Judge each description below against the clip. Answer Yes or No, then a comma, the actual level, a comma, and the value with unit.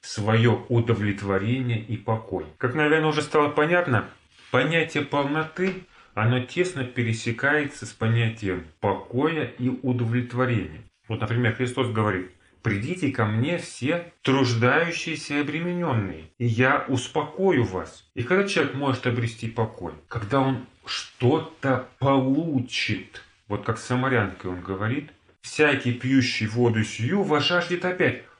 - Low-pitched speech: Yes, low, 125 Hz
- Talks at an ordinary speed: Yes, average, 120 wpm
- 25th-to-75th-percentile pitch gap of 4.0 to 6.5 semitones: Yes, average, 4.6 semitones